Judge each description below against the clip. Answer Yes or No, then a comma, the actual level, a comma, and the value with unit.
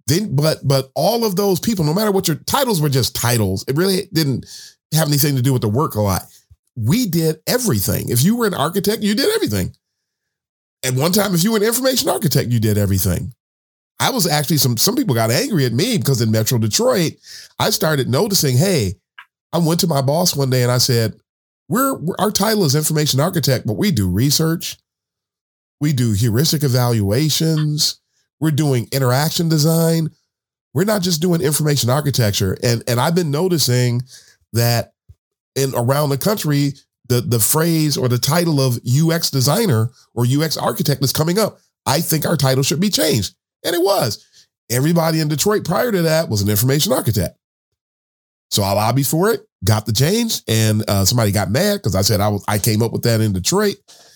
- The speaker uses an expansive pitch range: Yes, wide, 5.8 semitones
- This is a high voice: No, medium, 140 Hz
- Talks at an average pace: Yes, average, 190 wpm